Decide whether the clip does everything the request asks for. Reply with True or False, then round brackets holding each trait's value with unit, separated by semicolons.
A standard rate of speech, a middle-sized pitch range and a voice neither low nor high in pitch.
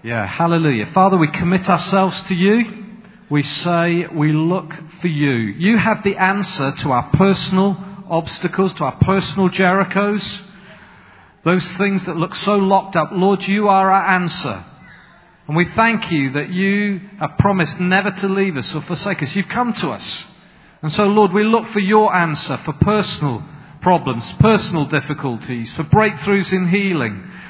True (160 wpm; 4.1 semitones; 180 Hz)